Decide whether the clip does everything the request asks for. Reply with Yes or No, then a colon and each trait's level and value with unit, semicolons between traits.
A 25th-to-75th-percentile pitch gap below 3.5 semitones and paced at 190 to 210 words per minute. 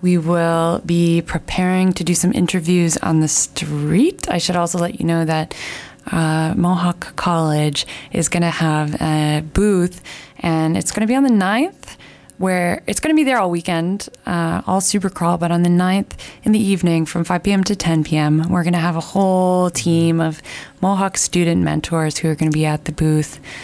Yes: narrow, 2.4 semitones; average, 200 wpm